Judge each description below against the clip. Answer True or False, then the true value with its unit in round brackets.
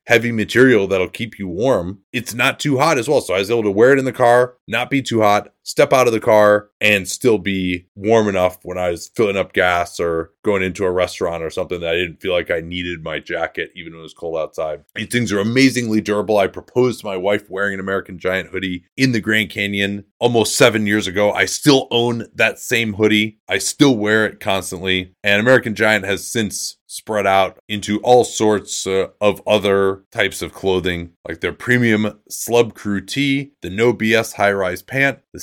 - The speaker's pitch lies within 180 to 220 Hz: False (105 Hz)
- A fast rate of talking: True (215 wpm)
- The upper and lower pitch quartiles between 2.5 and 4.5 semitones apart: True (3.3 semitones)